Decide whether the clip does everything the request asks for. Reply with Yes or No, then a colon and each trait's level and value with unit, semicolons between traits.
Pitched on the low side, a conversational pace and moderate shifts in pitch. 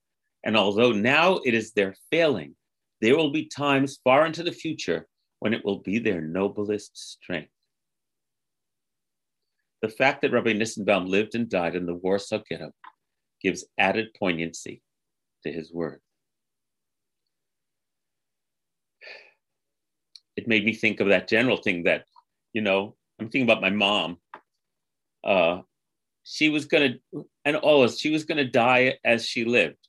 Yes: low, 110 Hz; average, 145 wpm; average, 4.9 semitones